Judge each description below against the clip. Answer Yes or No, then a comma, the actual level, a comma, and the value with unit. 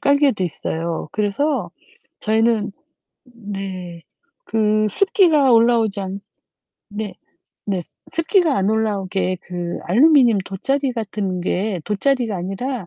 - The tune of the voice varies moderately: Yes, average, 4.6 semitones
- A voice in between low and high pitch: No, high, 215 Hz